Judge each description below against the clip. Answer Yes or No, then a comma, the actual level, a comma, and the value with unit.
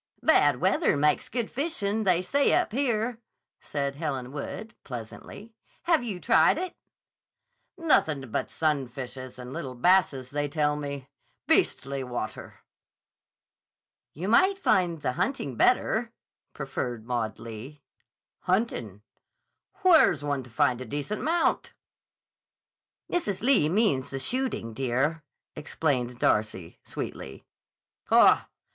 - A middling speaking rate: No, slow, 115 wpm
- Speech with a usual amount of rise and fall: No, wide, 9.0 semitones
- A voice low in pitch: No, medium, 145 Hz